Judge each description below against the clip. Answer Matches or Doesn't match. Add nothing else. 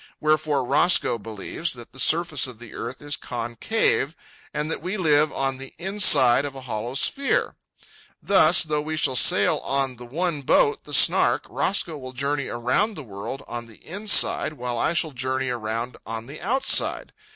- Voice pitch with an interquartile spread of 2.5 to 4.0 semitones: Doesn't match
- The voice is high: Doesn't match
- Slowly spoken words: Doesn't match